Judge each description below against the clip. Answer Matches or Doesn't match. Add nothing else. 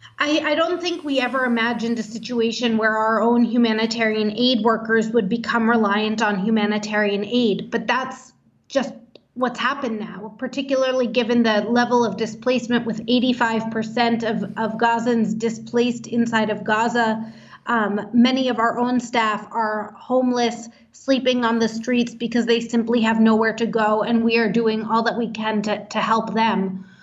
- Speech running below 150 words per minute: Doesn't match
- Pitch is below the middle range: Doesn't match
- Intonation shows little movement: Matches